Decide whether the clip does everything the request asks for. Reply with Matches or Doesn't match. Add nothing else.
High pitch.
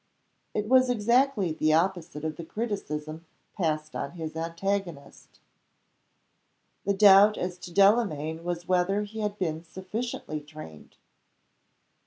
Doesn't match